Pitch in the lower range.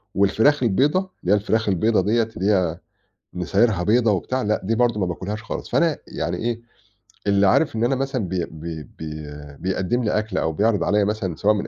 Yes: low, 105 Hz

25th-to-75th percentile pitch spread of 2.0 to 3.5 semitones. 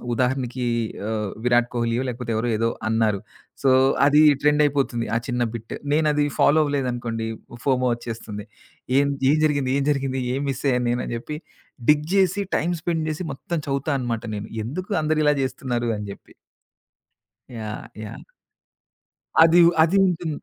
No: average, 4.0 semitones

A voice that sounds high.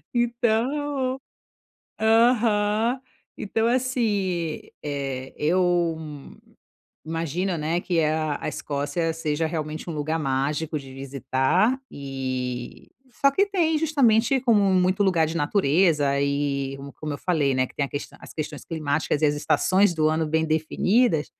No: medium, 160 Hz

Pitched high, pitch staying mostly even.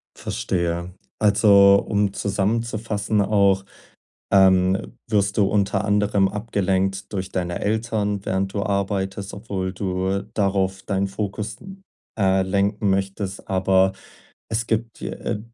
No: low, 100 Hz; narrow, 1.3 semitones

